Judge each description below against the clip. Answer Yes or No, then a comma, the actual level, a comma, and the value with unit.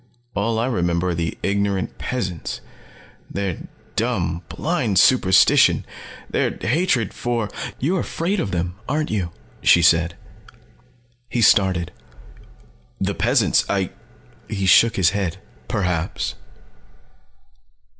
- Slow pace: Yes, slow, 115 wpm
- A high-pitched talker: No, low, 100 Hz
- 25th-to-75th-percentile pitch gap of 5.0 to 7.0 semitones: Yes, average, 5.3 semitones